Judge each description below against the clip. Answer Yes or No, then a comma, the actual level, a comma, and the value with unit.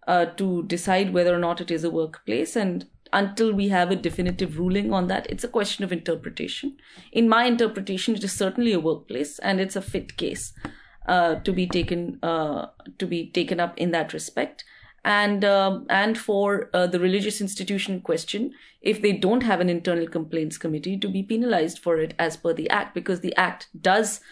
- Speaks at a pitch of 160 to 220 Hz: Yes, medium, 185 Hz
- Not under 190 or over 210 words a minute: Yes, average, 195 wpm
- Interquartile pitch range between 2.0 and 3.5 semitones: Yes, average, 3.0 semitones